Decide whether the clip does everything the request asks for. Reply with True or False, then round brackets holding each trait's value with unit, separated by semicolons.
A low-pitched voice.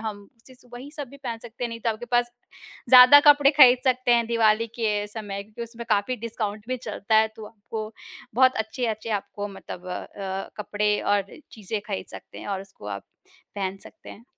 False (220 Hz)